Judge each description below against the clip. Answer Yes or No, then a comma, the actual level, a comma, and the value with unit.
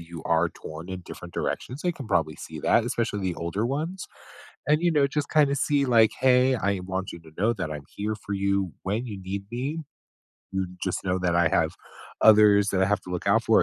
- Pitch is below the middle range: Yes, low, 100 Hz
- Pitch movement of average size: No, wide, 5.7 semitones